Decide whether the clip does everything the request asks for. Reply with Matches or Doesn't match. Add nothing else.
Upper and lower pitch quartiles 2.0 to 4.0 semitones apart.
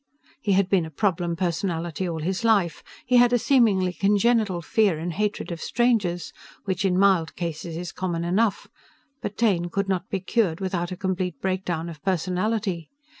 Matches